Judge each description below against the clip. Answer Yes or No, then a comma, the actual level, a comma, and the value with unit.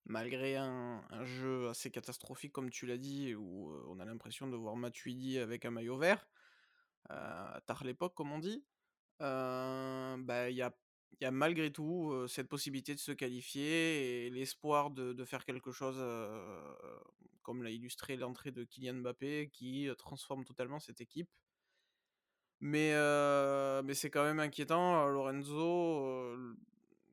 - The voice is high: No, low, 130 Hz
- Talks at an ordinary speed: Yes, average, 155 wpm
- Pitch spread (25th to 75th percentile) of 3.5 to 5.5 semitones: No, average, 2.8 semitones